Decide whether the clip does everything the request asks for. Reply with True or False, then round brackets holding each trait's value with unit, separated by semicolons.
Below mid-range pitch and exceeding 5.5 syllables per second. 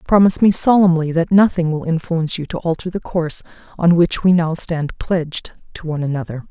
False (170 Hz; 5.9 syllables/s)